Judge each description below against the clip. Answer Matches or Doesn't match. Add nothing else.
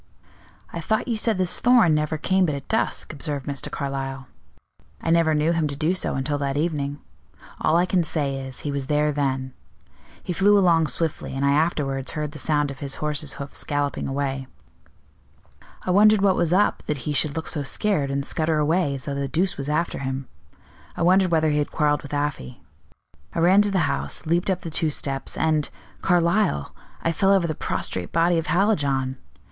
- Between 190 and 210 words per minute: Matches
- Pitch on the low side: Doesn't match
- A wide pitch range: Doesn't match